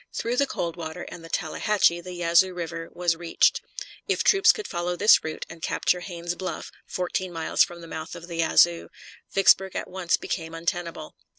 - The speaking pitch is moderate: Yes, medium, 175 Hz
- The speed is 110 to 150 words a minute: No, average, 180 wpm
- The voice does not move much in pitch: Yes, narrow, 1.6 semitones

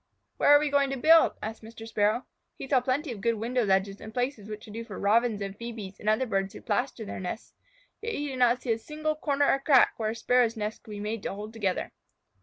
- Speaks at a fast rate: Yes, fast, 255 wpm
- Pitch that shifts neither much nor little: Yes, average, 3.8 semitones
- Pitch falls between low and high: No, high, 230 Hz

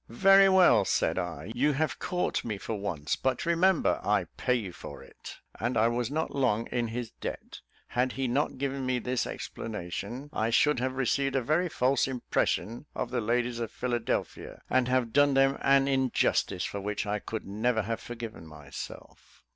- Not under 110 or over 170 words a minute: No, average, 180 wpm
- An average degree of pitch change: Yes, average, 3.4 semitones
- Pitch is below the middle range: Yes, low, 125 Hz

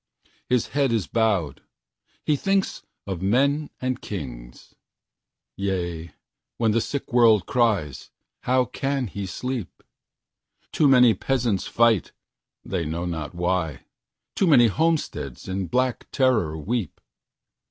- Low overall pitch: Yes, low, 110 Hz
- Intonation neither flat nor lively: No, wide, 6.5 semitones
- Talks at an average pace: No, slow, 110 wpm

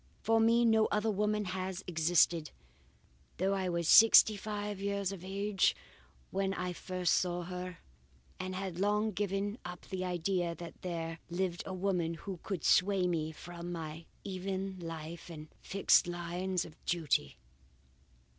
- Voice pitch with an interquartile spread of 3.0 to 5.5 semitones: No, narrow, 2.4 semitones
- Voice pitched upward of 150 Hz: Yes, medium, 185 Hz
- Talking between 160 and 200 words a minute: No, average, 150 wpm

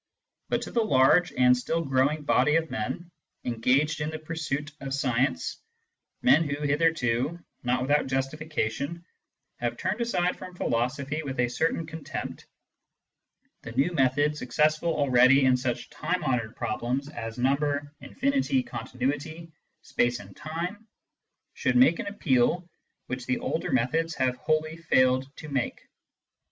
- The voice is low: No, medium, 145 Hz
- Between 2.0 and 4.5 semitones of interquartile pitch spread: Yes, average, 4.1 semitones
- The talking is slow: No, average, 145 wpm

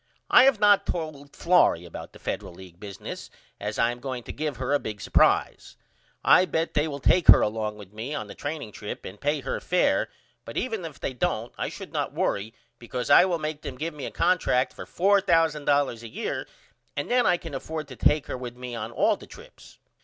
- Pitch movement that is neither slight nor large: No, wide, 5.9 semitones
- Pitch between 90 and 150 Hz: Yes, medium, 140 Hz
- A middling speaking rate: No, fast, 220 wpm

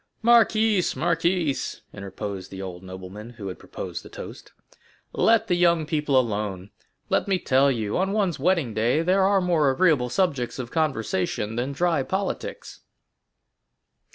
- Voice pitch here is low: No, medium, 145 Hz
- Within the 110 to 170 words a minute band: Yes, average, 145 wpm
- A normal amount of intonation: No, wide, 8.7 semitones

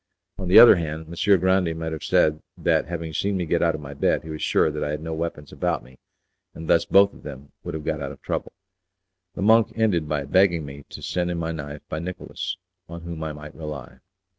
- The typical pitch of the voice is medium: No, very low, 80 Hz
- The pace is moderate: No, fast, 240 wpm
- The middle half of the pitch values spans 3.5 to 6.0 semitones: No, average, 2.7 semitones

